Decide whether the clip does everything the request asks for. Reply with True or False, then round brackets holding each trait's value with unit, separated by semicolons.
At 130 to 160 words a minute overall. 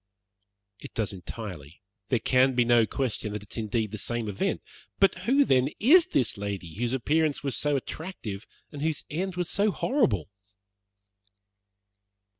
True (155 wpm)